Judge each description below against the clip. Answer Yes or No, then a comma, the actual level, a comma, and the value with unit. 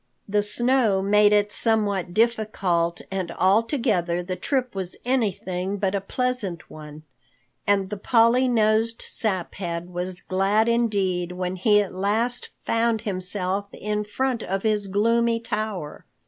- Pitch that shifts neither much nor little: Yes, average, 3.6 semitones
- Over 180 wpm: No, slow, 135 wpm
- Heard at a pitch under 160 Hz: No, high, 205 Hz